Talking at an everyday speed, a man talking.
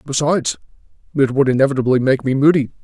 Yes: average, 150 wpm; male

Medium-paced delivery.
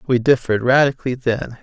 Yes: average, 145 wpm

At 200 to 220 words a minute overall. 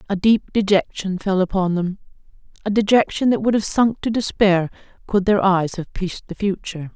No: average, 175 wpm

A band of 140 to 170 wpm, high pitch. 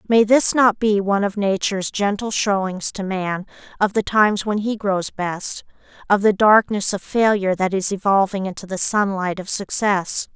No: average, 180 wpm; high, 200 Hz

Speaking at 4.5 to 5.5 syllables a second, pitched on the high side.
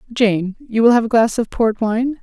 Yes: 4.7 syllables/s; high, 225 Hz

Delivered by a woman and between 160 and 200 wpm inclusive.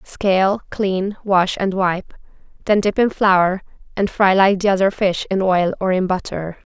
Yes: female; average, 180 wpm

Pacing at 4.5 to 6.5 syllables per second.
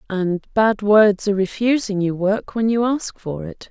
No: 4.3 syllables/s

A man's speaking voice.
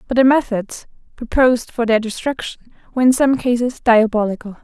No: female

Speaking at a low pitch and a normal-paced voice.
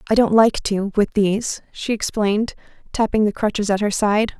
No: high, 210 Hz; average, 175 wpm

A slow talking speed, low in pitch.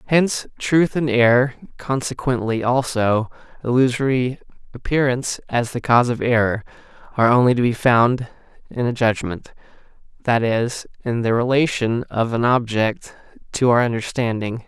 Yes: slow, 130 wpm; low, 120 Hz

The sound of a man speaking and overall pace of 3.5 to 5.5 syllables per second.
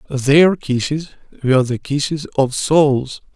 Yes: male; 3.9 syllables/s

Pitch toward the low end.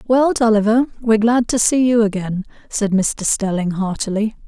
No: high, 220 Hz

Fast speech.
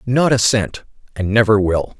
No: average, 180 wpm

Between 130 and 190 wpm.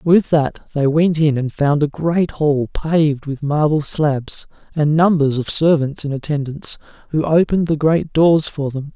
Yes: average, 180 wpm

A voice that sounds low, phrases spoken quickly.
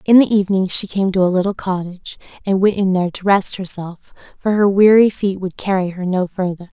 No: high, 190 Hz; fast, 220 wpm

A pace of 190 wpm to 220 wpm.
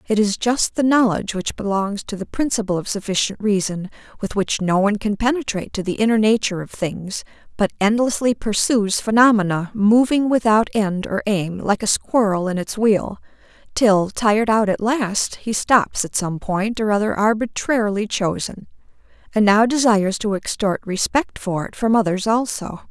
No: average, 170 wpm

